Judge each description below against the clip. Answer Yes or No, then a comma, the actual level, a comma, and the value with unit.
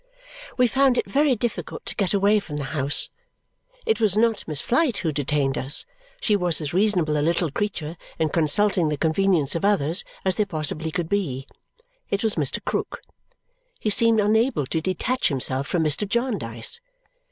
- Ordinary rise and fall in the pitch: No, wide, 6.0 semitones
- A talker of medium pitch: Yes, medium, 180 Hz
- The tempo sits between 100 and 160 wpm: No, average, 175 wpm